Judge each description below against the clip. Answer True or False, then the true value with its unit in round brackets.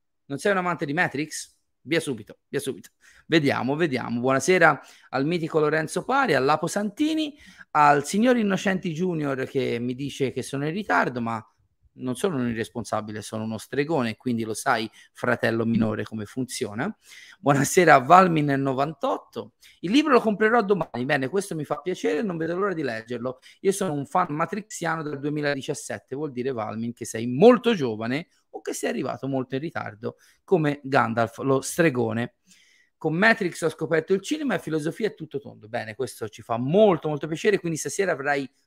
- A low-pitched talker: False (150 Hz)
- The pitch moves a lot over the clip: True (6.7 semitones)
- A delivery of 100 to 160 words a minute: False (170 wpm)